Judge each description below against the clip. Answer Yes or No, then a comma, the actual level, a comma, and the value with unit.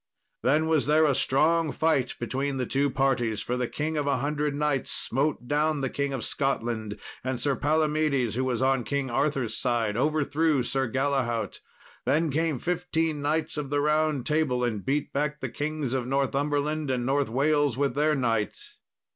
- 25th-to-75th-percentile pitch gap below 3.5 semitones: Yes, average, 2.8 semitones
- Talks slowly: No, average, 175 wpm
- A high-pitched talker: No, medium, 140 Hz